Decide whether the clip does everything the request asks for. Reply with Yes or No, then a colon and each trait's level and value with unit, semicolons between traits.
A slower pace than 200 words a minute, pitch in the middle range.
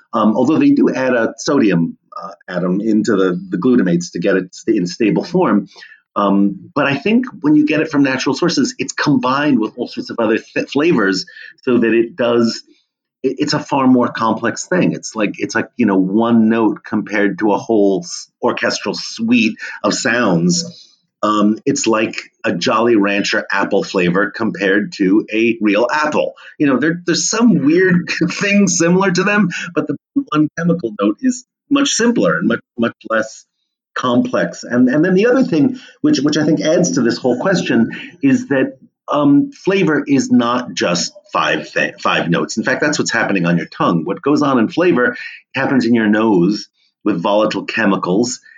Yes: average, 180 wpm; medium, 150 Hz